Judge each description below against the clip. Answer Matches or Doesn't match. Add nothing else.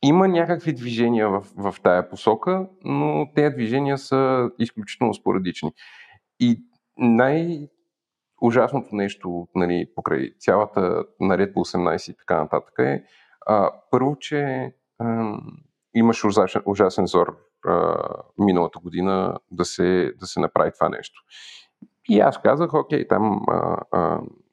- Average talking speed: Matches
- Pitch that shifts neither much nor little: Doesn't match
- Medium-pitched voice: Doesn't match